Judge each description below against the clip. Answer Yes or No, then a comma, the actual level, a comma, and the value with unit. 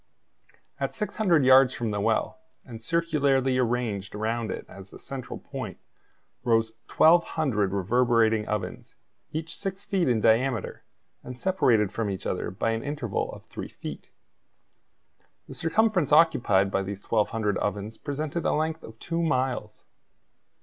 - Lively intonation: Yes, wide, 6.5 semitones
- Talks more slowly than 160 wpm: Yes, average, 140 wpm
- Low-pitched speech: Yes, low, 120 Hz